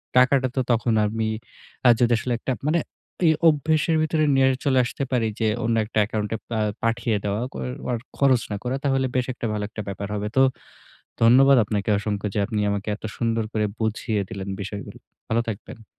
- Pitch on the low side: Yes, low, 115 Hz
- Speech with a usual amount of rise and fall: Yes, average, 3.5 semitones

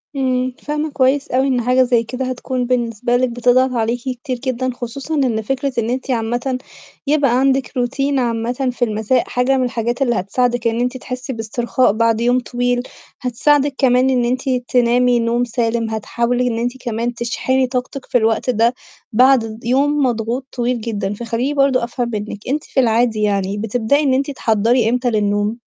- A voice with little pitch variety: Yes, narrow, 2.0 semitones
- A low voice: No, high, 245 Hz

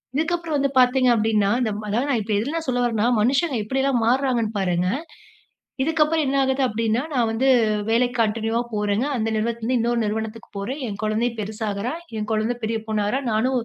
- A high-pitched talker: Yes, high, 230 Hz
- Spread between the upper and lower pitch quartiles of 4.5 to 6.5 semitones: No, average, 3.5 semitones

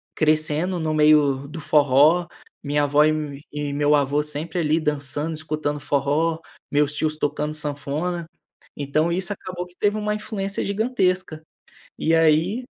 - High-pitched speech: No, medium, 155 Hz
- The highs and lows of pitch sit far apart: No, average, 3.0 semitones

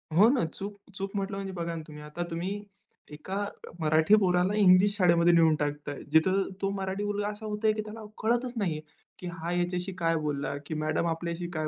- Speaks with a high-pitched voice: No, medium, 180 Hz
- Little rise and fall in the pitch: No, average, 3.8 semitones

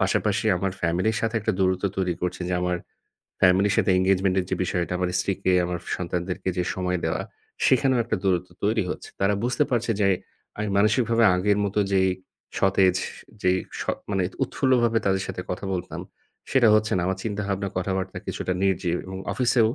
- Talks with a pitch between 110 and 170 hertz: No, very low, 95 Hz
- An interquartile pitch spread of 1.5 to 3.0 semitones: Yes, average, 2.7 semitones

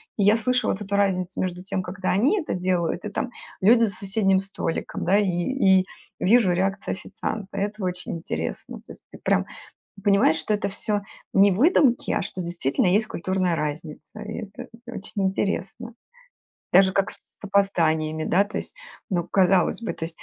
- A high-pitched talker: Yes, high, 195 Hz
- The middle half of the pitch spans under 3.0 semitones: Yes, narrow, 2.6 semitones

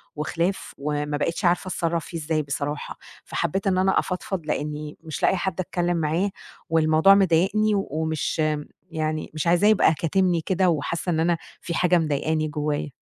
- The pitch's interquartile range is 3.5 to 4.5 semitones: No, average, 3.0 semitones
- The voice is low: No, medium, 165 Hz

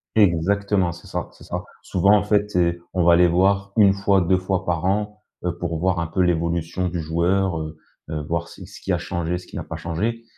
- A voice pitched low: Yes, very low, 90 Hz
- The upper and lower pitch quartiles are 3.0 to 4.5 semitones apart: No, narrow, 2.6 semitones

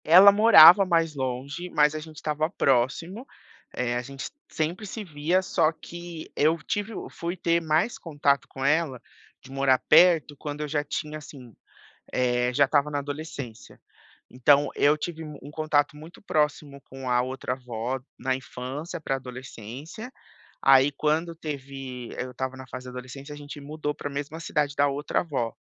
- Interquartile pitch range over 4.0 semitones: No, average, 3.3 semitones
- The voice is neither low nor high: Yes, medium, 145 Hz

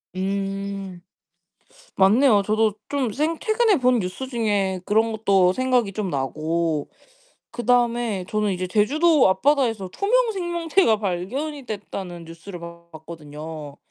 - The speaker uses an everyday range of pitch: No, wide, 5.9 semitones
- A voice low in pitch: No, high, 205 Hz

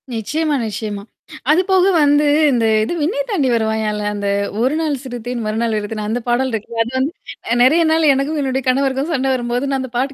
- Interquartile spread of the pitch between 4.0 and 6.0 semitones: Yes, average, 4.5 semitones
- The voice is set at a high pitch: Yes, very high, 260 Hz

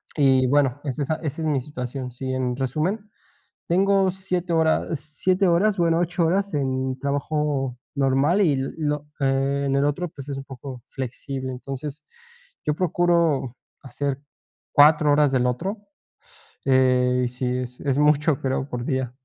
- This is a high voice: No, medium, 140 Hz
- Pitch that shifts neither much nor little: Yes, average, 3.6 semitones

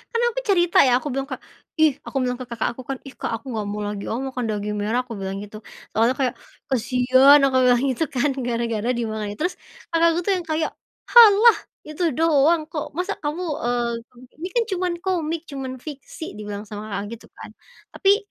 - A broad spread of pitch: Yes, wide, 5.8 semitones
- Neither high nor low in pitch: No, very high, 260 Hz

